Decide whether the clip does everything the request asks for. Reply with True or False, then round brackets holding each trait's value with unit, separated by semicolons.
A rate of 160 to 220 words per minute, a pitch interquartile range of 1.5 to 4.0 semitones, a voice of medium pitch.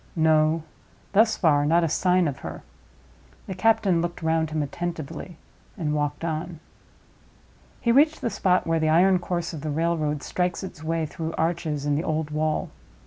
True (170 wpm; 2.5 semitones; 165 Hz)